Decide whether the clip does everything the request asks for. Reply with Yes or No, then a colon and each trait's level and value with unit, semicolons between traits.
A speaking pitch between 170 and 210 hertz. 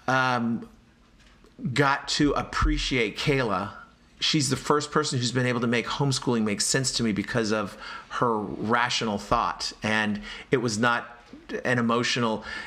No: low, 125 Hz